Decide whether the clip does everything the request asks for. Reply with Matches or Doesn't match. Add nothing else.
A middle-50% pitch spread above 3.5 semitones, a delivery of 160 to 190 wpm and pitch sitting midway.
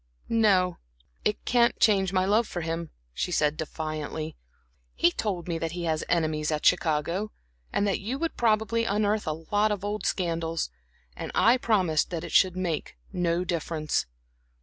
Matches